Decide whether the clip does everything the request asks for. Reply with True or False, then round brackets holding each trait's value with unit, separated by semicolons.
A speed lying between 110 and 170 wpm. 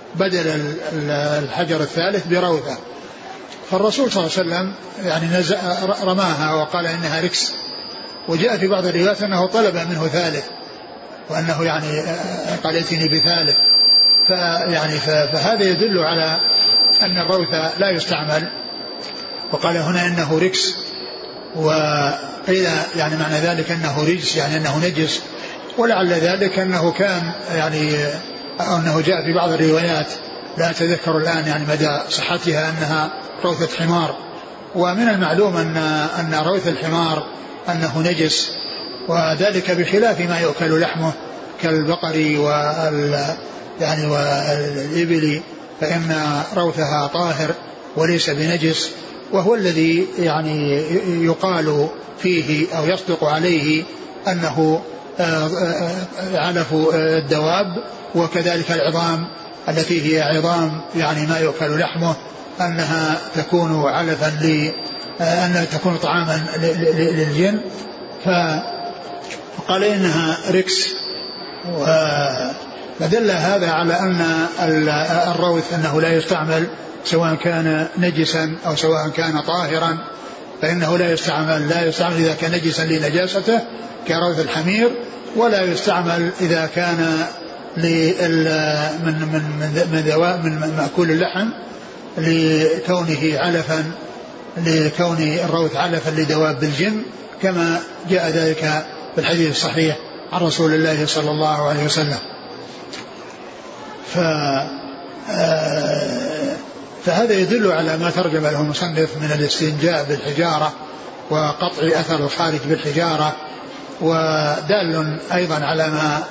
False (100 wpm)